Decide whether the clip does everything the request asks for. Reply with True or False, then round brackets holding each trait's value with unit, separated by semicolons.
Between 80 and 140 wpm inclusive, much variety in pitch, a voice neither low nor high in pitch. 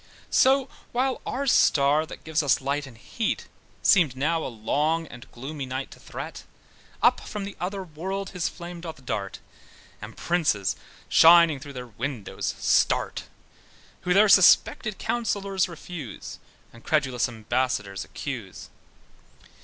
True (135 wpm; 6.1 semitones; 155 Hz)